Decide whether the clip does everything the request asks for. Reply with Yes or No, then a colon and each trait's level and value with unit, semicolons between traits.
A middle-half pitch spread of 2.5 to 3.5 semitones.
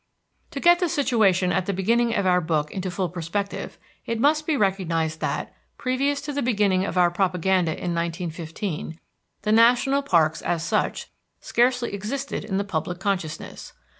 No: wide, 5.6 semitones